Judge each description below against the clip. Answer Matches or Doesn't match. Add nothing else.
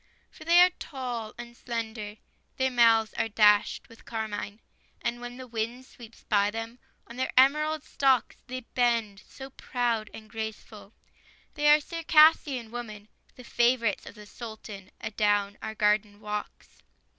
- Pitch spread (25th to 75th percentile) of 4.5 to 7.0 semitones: Doesn't match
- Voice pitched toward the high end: Matches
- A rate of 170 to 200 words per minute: Doesn't match